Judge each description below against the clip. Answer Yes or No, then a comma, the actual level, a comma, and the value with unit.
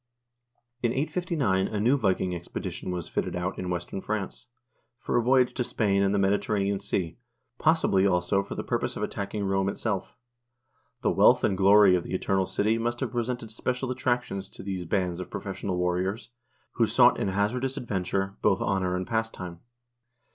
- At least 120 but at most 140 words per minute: No, average, 170 wpm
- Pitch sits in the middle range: No, low, 100 Hz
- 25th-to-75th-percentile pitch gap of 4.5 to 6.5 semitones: No, average, 4.1 semitones